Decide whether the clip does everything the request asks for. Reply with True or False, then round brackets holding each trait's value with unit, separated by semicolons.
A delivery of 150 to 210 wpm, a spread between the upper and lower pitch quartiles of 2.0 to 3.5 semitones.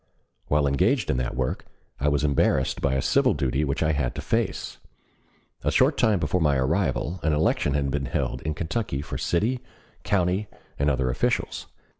False (180 wpm; 3.9 semitones)